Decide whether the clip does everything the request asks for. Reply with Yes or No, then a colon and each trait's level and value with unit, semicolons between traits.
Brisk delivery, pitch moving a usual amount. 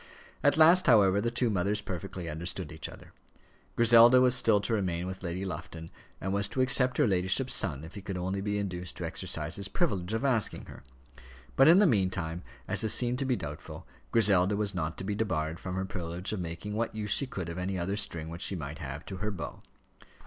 Yes: fast, 220 wpm; average, 4.1 semitones